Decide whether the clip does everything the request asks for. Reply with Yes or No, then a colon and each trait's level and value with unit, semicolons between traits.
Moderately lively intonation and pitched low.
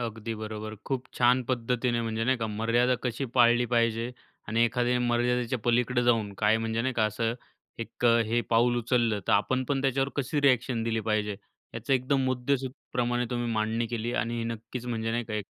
No: narrow, 1.6 semitones; low, 120 Hz